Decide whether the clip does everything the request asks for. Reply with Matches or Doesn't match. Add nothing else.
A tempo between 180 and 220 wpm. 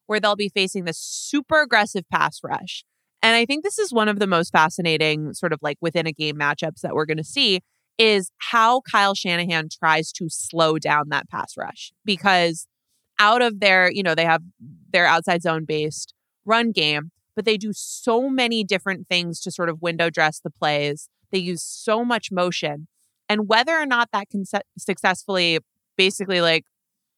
Matches